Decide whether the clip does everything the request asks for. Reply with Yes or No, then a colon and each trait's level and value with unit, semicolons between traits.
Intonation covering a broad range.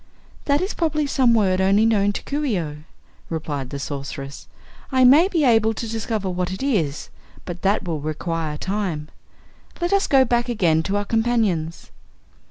Yes: wide, 6.8 semitones